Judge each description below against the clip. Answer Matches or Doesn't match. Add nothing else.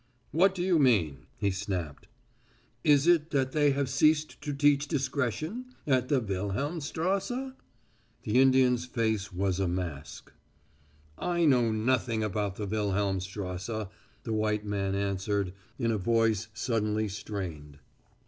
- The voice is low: Matches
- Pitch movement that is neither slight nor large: Doesn't match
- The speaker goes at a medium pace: Doesn't match